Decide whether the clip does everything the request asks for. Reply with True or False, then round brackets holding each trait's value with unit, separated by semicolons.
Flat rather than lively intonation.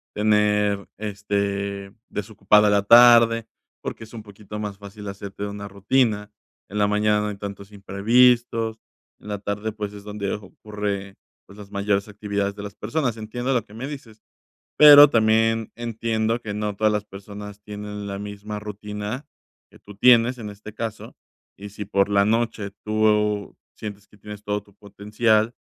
True (1.4 semitones)